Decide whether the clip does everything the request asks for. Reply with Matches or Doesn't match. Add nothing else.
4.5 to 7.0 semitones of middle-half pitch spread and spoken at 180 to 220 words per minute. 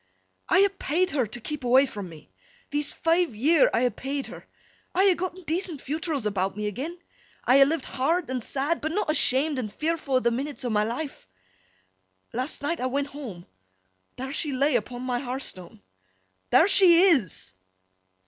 Matches